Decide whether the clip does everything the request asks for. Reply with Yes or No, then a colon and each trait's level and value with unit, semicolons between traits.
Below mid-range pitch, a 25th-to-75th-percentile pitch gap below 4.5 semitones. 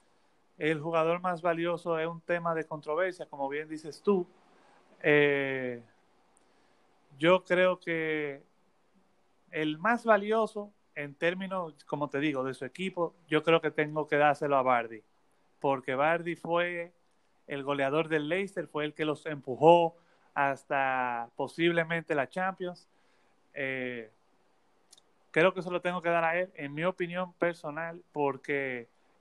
No: medium, 160 Hz; average, 3.6 semitones